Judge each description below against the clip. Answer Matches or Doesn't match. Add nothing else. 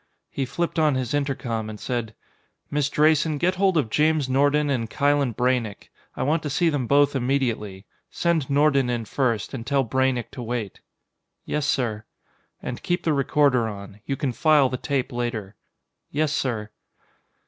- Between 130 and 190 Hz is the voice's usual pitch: Matches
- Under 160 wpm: Doesn't match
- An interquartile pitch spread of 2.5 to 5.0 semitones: Matches